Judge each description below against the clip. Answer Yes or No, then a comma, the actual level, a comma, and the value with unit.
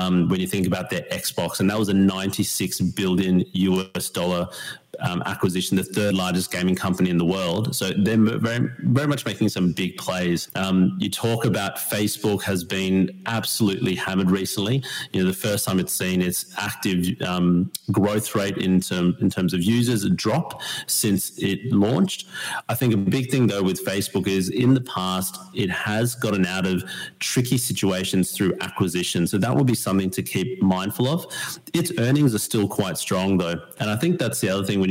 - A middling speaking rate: Yes, average, 185 wpm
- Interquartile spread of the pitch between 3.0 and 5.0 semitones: Yes, average, 3.3 semitones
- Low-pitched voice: Yes, very low, 95 Hz